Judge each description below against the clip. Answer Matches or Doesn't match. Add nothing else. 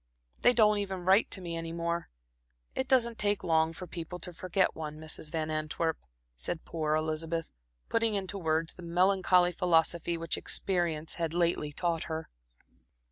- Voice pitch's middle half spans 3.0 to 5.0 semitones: Doesn't match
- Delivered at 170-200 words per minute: Doesn't match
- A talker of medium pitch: Matches